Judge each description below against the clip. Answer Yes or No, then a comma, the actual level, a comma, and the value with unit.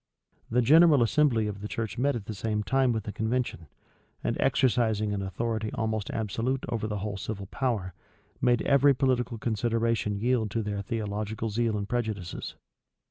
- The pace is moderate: Yes, average, 165 wpm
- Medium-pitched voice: No, low, 110 Hz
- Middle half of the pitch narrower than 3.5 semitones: Yes, average, 2.7 semitones